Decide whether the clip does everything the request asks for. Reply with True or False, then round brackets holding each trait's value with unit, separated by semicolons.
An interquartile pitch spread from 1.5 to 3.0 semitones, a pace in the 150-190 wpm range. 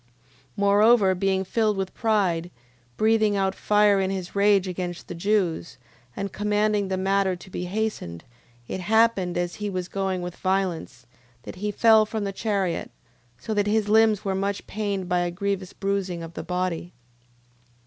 True (2.5 semitones; 170 wpm)